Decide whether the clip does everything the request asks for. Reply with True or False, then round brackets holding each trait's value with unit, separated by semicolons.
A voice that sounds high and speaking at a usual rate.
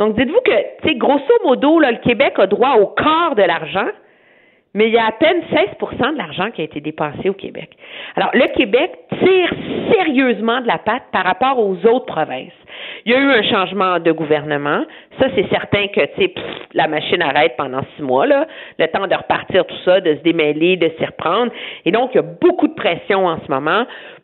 True (225 Hz; 210 wpm)